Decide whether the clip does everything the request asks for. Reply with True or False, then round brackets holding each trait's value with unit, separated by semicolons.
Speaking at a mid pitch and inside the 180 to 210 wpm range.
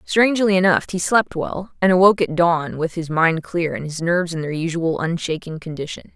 True (170 Hz; 205 wpm)